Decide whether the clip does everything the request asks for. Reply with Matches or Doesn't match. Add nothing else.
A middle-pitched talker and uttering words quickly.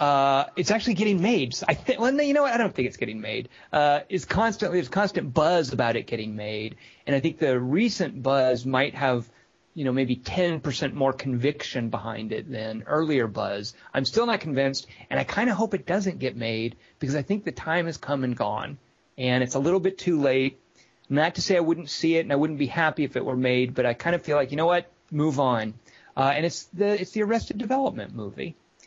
Matches